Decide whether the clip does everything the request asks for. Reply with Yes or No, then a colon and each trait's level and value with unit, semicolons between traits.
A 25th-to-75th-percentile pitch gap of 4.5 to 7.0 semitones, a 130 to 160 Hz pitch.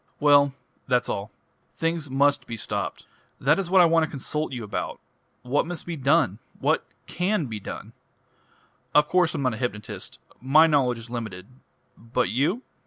Yes: average, 5.1 semitones; medium, 140 Hz